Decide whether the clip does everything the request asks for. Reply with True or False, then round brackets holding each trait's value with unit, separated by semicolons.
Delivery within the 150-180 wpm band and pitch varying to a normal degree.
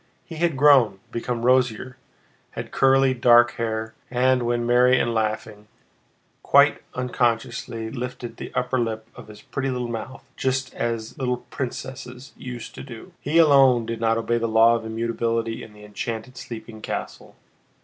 False (160 wpm; 2.2 semitones)